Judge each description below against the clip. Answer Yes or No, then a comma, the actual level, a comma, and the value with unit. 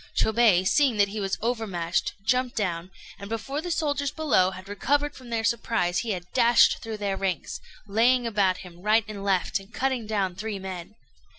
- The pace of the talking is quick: No, average, 185 wpm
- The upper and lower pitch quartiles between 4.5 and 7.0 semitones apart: No, average, 3.9 semitones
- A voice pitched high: Yes, high, 215 Hz